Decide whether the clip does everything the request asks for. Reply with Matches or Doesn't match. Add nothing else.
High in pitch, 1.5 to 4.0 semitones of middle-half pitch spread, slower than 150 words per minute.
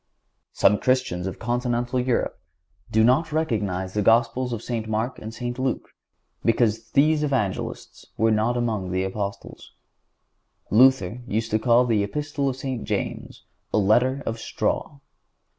Doesn't match